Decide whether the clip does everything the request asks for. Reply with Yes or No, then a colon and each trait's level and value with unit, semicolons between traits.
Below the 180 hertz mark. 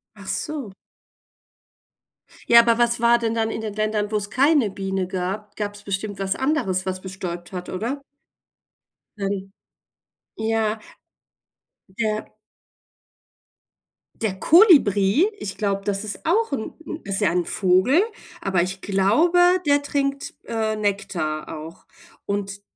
No: high, 205 Hz